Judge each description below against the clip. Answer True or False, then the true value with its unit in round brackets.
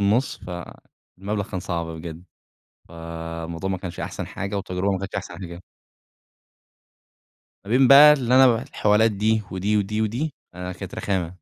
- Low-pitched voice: True (95 Hz)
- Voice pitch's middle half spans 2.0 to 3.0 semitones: False (3.9 semitones)